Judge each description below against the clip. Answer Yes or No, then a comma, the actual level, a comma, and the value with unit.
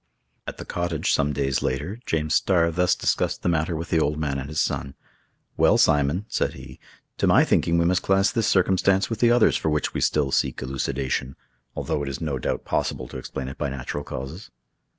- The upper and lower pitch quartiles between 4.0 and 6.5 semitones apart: Yes, average, 4.6 semitones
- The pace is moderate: No, fast, 210 wpm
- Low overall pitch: Yes, very low, 75 Hz